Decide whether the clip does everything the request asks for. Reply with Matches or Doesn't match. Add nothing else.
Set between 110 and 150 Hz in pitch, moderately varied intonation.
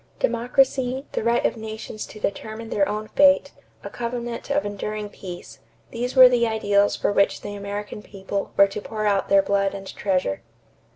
Doesn't match